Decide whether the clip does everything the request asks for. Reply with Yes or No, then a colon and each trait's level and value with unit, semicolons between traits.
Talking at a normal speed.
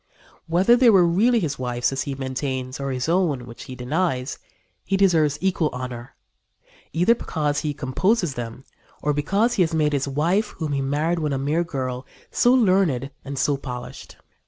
Yes: average, 180 wpm